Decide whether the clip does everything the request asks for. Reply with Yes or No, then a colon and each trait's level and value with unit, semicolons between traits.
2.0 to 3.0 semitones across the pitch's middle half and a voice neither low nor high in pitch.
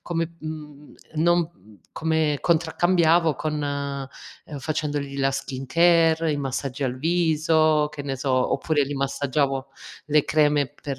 Yes: narrow, 2.5 semitones; medium, 150 Hz